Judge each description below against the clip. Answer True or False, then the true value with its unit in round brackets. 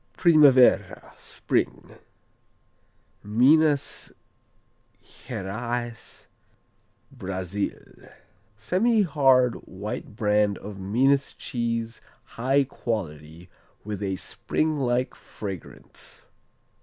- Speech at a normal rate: False (65 wpm)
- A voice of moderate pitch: False (115 Hz)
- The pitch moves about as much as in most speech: True (4.9 semitones)